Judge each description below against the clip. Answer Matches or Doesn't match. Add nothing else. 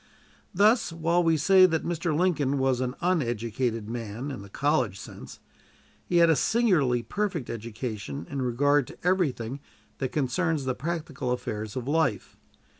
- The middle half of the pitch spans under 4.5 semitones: Doesn't match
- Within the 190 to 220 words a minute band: Doesn't match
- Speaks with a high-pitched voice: Doesn't match